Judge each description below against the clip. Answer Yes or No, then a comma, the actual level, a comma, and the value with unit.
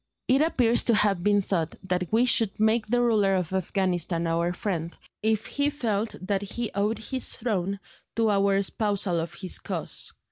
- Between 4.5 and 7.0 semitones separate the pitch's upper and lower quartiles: No, average, 3.5 semitones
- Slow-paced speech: No, average, 175 wpm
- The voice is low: No, high, 200 Hz